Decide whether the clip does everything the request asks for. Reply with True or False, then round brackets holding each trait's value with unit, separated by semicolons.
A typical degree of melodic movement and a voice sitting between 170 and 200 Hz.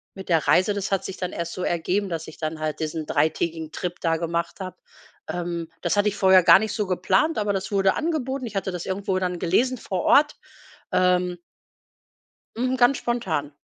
True (3.3 semitones; 185 Hz)